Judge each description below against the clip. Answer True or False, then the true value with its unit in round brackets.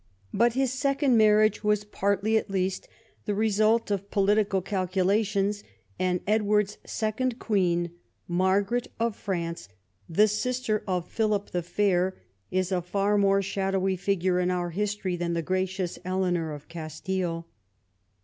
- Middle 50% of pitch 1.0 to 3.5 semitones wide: True (2.7 semitones)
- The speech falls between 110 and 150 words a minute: True (135 wpm)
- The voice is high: True (195 Hz)